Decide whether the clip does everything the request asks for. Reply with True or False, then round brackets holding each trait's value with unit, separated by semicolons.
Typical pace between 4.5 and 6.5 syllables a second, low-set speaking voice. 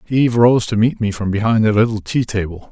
True (5.9 syllables/s; 110 Hz)